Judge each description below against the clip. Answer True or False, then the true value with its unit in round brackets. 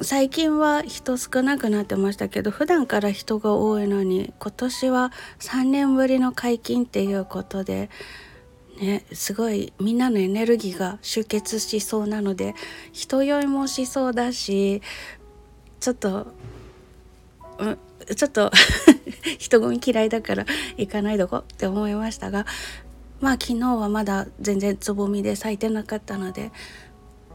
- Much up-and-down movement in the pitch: False (4.1 semitones)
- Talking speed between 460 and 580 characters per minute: False (270 characters per minute)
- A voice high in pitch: True (220 Hz)